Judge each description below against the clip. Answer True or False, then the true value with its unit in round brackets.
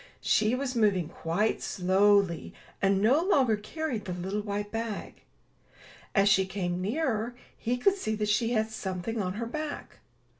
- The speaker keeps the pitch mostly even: False (3.4 semitones)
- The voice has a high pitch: True (210 Hz)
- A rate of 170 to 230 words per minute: False (155 wpm)